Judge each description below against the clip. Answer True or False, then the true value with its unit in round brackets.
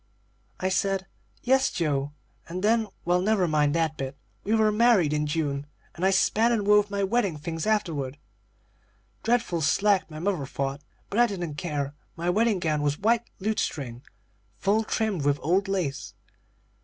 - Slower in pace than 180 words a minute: True (160 wpm)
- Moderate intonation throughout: False (5.9 semitones)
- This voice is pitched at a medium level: True (180 Hz)